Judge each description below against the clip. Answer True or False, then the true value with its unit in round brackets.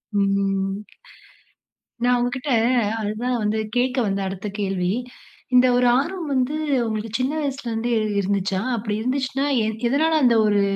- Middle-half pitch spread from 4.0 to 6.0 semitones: True (4.4 semitones)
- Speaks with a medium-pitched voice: False (235 Hz)